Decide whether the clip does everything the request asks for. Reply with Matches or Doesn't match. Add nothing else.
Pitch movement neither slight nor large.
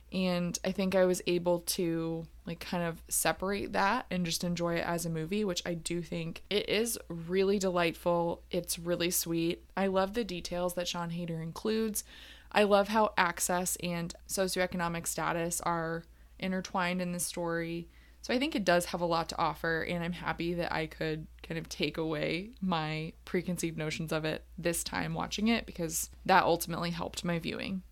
Doesn't match